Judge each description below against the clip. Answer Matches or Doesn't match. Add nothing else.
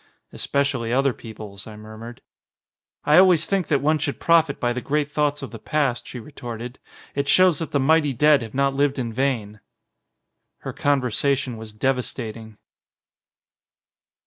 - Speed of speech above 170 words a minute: Doesn't match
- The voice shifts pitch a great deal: Doesn't match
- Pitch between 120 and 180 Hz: Matches